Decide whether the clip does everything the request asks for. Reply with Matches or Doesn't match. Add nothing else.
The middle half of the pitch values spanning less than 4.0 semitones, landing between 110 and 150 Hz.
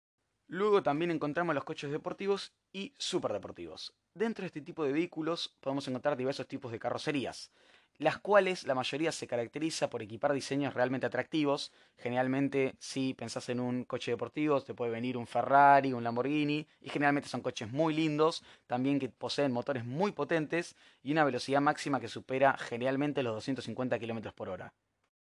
Matches